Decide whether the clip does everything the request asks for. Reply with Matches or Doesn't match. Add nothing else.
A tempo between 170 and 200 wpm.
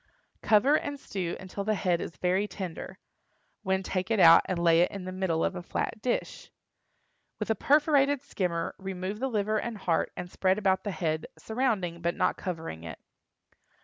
Matches